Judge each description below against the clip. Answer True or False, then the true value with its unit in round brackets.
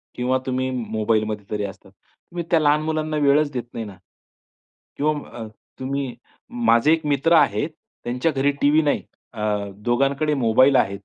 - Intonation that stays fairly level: False (5.2 semitones)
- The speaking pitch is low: True (130 Hz)